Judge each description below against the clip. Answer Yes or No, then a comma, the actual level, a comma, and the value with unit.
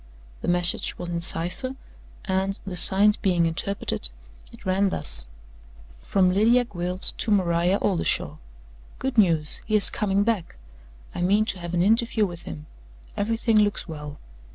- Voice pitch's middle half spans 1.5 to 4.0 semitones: Yes, average, 3.4 semitones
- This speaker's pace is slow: No, average, 150 wpm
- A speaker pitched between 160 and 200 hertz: Yes, high, 190 Hz